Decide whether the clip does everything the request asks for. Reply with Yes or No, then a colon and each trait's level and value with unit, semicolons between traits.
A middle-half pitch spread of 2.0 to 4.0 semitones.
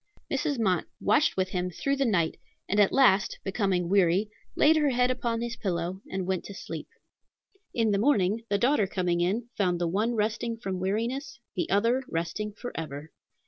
No: average, 4.5 semitones